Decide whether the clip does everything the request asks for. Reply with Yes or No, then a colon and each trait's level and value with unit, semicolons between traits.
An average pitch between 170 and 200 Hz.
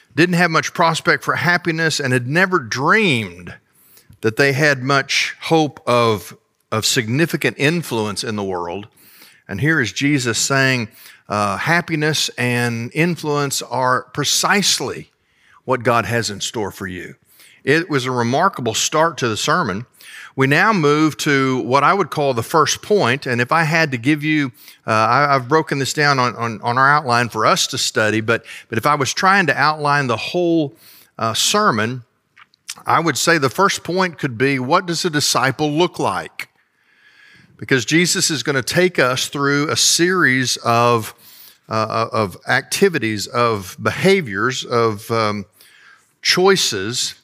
No: medium, 140 Hz